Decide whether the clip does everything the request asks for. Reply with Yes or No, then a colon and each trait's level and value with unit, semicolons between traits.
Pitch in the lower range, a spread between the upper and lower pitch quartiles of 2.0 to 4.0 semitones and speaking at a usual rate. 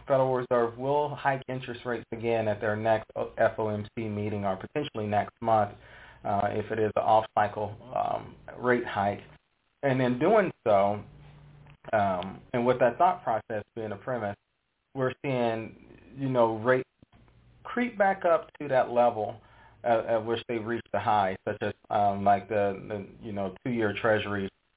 Yes: low, 115 Hz; average, 3.5 semitones; average, 160 wpm